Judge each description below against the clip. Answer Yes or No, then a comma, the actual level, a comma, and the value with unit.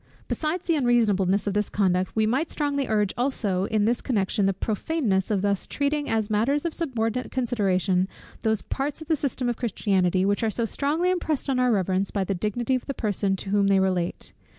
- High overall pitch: Yes, high, 220 Hz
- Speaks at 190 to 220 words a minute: Yes, average, 200 wpm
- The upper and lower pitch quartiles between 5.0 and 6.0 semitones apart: Yes, wide, 5.5 semitones